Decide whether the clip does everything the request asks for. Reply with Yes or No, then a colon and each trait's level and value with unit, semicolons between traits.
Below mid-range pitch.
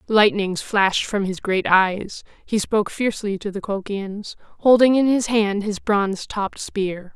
No: high, 205 Hz